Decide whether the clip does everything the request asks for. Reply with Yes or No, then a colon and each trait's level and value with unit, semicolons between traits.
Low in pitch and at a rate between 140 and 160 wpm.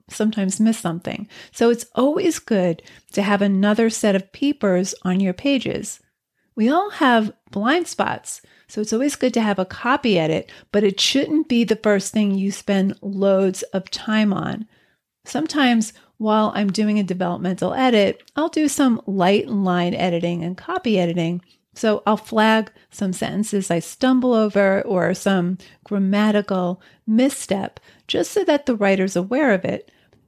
No: high, 210 Hz; average, 155 wpm